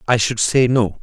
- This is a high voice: No, low, 115 Hz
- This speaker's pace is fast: Yes, fast, 235 wpm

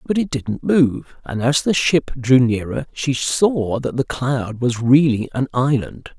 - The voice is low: Yes, low, 130 Hz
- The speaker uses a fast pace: No, average, 185 wpm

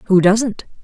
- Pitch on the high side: Yes, high, 205 Hz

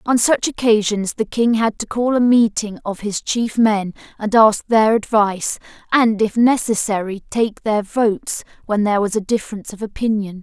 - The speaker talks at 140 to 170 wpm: No, average, 180 wpm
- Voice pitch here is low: No, high, 215 Hz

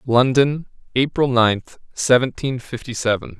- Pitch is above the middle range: No, low, 125 Hz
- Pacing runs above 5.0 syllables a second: No, 4.2 syllables/s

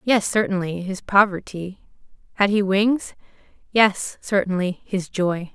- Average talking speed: No, slow, 120 wpm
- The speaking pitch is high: Yes, high, 195 Hz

